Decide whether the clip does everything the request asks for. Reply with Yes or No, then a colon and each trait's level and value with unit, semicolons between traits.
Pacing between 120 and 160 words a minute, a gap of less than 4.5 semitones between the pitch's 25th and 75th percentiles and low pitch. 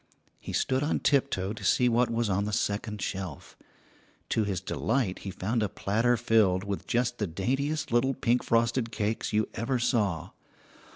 No: average, 170 wpm; average, 3.3 semitones; low, 115 Hz